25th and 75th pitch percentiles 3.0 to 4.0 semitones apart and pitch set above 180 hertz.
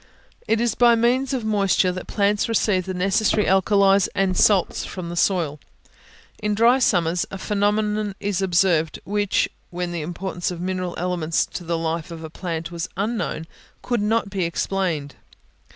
Yes: average, 3.3 semitones; high, 190 Hz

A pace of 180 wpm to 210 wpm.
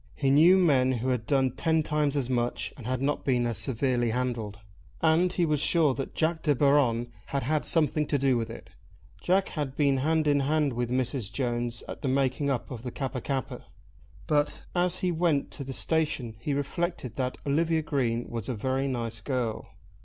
Yes: average, 200 wpm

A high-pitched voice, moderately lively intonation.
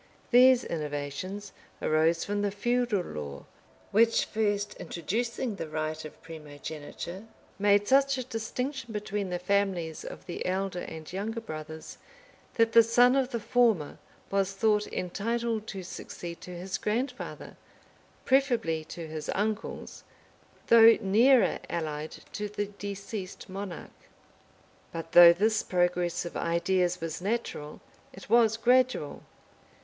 Yes: high, 200 Hz; average, 5.0 semitones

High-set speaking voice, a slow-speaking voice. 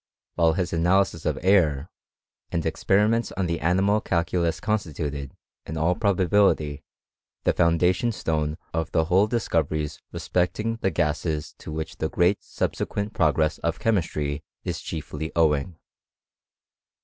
No: very low, 85 Hz; slow, 125 wpm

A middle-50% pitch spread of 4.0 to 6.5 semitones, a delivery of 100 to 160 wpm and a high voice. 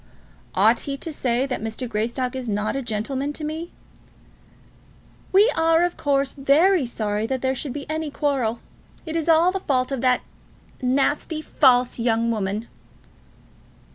Yes: average, 4.6 semitones; average, 155 wpm; very high, 270 Hz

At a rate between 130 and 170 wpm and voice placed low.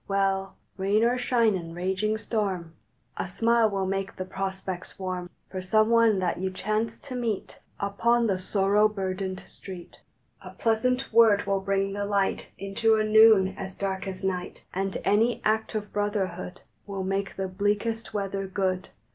No: average, 165 wpm; high, 195 Hz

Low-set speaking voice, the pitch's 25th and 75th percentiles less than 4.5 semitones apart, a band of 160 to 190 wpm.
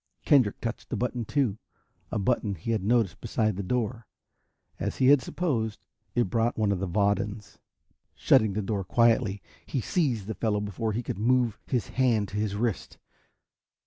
Yes: low, 110 Hz; average, 3.1 semitones; average, 175 wpm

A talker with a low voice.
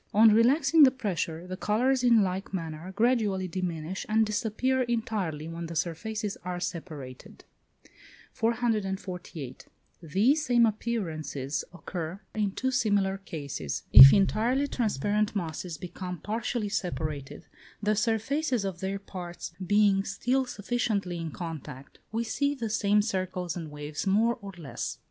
No: high, 195 Hz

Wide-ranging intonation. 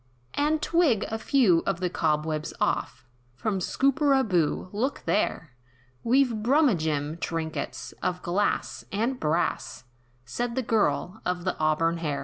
Yes: wide, 7.1 semitones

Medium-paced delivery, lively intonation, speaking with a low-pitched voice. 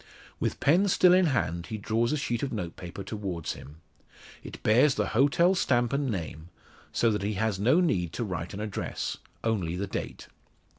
Yes: average, 185 wpm; wide, 6.9 semitones; low, 110 Hz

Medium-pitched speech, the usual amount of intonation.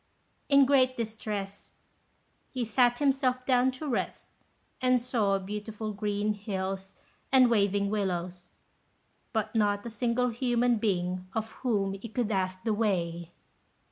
No: high, 215 Hz; average, 3.9 semitones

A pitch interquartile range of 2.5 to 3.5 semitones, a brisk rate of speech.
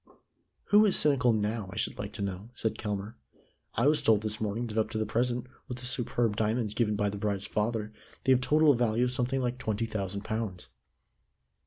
Yes: average, 2.9 semitones; fast, 210 wpm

